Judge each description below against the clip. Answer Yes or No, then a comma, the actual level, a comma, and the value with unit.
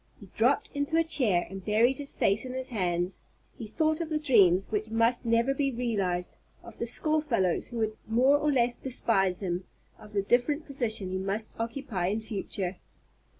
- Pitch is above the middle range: Yes, high, 230 Hz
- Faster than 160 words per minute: Yes, average, 190 wpm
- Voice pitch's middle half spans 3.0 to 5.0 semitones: No, wide, 5.6 semitones